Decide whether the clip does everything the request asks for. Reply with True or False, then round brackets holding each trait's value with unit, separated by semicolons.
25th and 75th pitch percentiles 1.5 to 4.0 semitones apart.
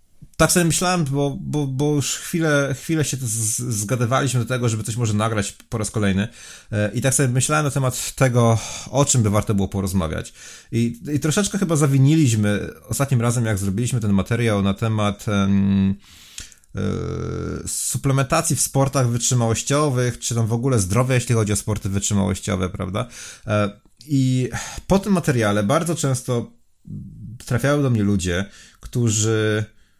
False (4.7 semitones)